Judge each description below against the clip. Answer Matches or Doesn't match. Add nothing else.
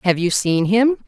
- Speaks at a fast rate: Matches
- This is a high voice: Matches